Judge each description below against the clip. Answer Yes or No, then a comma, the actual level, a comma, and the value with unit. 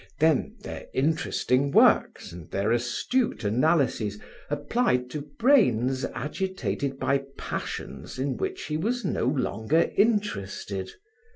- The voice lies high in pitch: No, medium, 140 Hz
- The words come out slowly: Yes, slow, 110 wpm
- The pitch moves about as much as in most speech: No, wide, 6.3 semitones